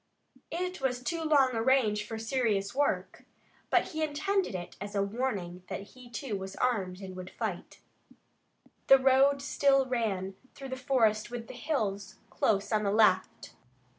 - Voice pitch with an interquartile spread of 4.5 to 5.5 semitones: Yes, average, 5.2 semitones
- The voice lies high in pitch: Yes, high, 235 Hz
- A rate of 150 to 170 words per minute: Yes, average, 165 wpm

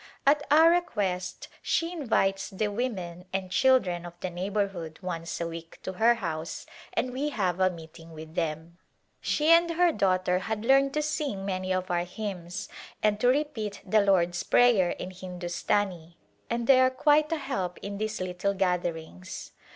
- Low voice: No, high, 195 Hz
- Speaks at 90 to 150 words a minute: No, average, 165 wpm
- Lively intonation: Yes, wide, 5.7 semitones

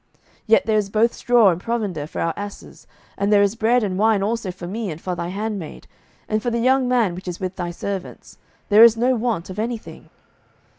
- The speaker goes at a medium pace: No, fast, 230 wpm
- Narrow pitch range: No, average, 3.7 semitones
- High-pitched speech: Yes, high, 210 Hz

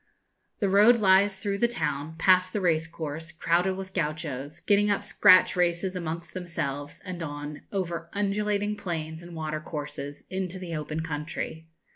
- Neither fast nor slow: Yes, average, 155 wpm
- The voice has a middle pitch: Yes, medium, 170 Hz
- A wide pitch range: No, average, 3.5 semitones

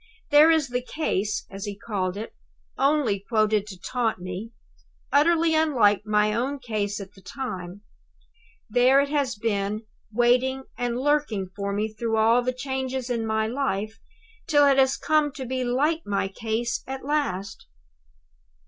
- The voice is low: No, high, 235 Hz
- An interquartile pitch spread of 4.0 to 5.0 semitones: Yes, average, 4.5 semitones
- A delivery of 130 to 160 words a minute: Yes, average, 155 wpm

